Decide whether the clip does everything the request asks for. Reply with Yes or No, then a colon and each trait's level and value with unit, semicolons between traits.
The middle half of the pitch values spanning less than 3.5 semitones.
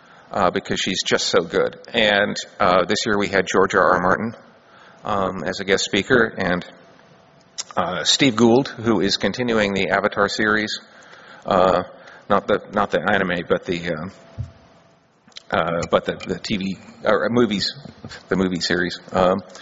Yes: average, 3.1 semitones